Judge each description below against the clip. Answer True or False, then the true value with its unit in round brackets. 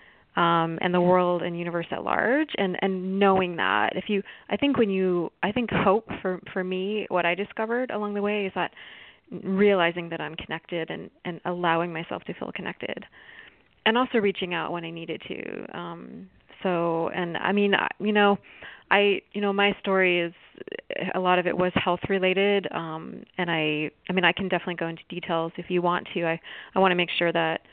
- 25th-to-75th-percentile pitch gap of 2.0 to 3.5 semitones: True (2.8 semitones)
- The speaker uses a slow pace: False (200 wpm)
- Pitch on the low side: False (180 Hz)